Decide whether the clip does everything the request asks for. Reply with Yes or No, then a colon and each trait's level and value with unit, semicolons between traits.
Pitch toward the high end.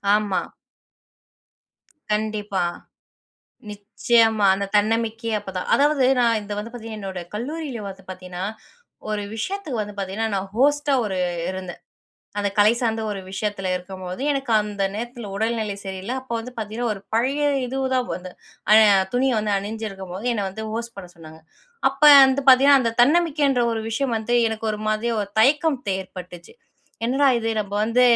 Yes: high, 220 Hz